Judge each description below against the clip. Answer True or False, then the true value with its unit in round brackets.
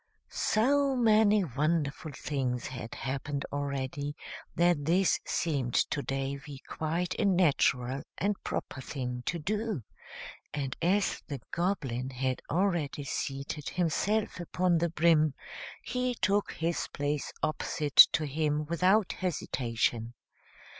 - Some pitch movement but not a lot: True (5.0 semitones)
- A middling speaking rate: False (115 wpm)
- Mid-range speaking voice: True (150 Hz)